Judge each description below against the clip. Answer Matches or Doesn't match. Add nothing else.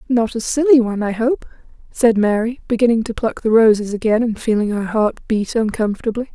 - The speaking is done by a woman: Matches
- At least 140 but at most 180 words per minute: Doesn't match